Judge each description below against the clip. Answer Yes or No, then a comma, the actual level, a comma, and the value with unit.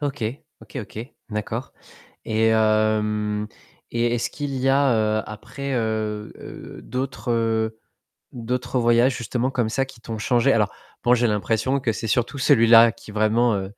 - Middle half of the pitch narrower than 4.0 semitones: Yes, narrow, 2.5 semitones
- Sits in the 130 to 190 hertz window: No, low, 115 Hz